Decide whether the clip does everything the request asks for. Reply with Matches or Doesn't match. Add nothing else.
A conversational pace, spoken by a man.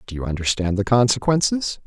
Matches